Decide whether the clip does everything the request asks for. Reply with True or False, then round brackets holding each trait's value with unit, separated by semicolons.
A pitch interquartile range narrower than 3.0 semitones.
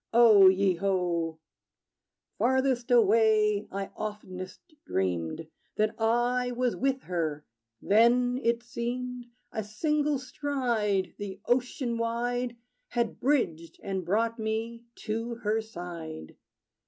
False (4.0 semitones)